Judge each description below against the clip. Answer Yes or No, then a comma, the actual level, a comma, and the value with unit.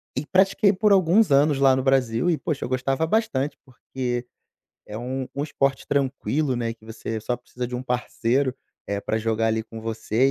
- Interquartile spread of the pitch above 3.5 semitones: Yes, average, 3.9 semitones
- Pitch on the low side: Yes, low, 130 Hz